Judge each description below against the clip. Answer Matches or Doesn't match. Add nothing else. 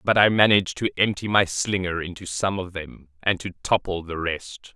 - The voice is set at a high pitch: Doesn't match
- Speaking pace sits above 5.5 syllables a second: Doesn't match